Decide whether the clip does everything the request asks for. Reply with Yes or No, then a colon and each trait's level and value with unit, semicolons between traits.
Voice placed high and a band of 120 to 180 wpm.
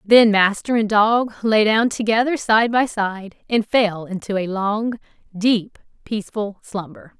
Yes: high, 210 Hz; average, 150 wpm